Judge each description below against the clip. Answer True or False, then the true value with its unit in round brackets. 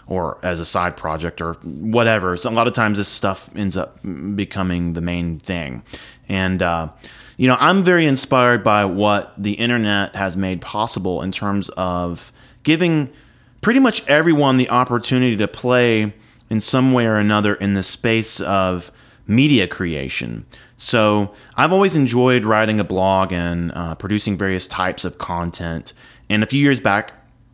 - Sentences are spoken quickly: False (165 wpm)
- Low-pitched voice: True (105 Hz)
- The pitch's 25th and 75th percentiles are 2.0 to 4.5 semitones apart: False (4.9 semitones)